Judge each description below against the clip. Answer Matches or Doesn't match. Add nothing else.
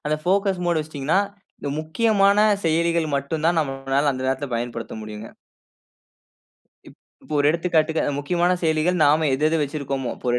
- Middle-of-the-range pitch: Matches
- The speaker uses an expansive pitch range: Doesn't match